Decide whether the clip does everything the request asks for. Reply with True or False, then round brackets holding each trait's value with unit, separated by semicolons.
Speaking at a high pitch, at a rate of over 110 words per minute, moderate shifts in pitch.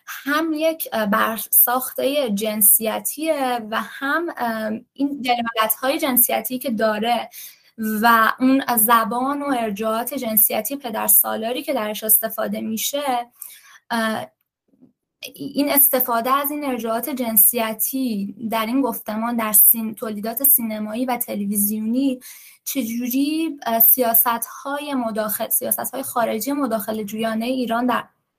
False (235 Hz; 105 wpm; 3.2 semitones)